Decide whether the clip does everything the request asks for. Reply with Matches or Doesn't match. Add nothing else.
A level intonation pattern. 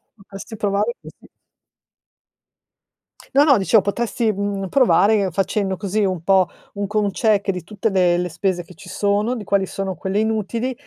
Matches